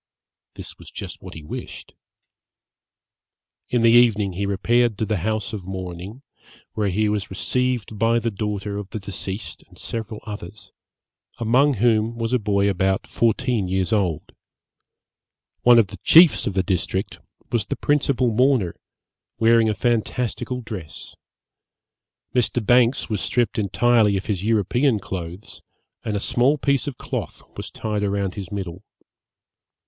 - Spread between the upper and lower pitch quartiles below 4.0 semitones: Yes, average, 3.4 semitones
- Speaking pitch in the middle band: No, low, 110 Hz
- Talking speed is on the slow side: No, average, 145 wpm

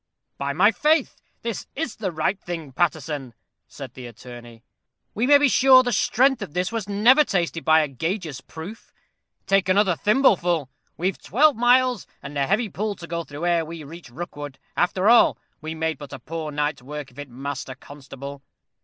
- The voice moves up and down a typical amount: No, wide, 6.6 semitones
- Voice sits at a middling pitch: Yes, medium, 170 Hz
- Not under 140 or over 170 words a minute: No, average, 180 wpm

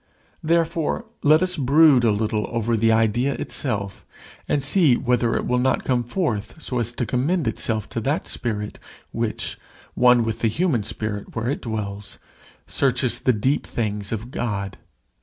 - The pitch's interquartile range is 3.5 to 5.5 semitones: Yes, average, 4.0 semitones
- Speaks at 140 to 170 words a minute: Yes, average, 160 wpm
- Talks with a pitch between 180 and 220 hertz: No, low, 120 Hz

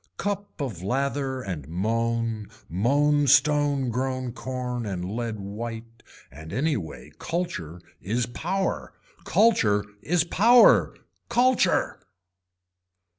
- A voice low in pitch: Yes, low, 125 Hz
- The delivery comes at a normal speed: No, slow, 100 wpm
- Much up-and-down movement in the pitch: Yes, wide, 5.8 semitones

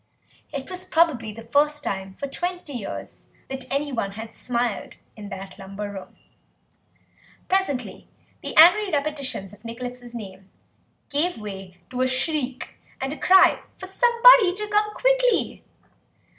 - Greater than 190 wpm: No, slow, 135 wpm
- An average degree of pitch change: No, wide, 8.5 semitones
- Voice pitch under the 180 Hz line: No, very high, 265 Hz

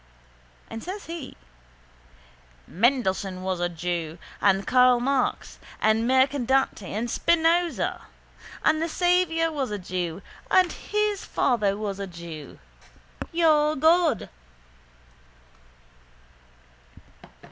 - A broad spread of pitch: Yes, wide, 8.9 semitones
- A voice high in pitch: Yes, very high, 250 Hz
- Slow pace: Yes, slow, 95 wpm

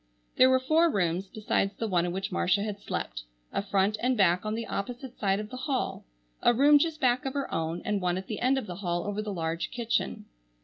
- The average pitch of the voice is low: No, high, 210 Hz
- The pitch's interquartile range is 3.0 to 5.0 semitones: No, wide, 5.4 semitones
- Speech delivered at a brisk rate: Yes, fast, 235 wpm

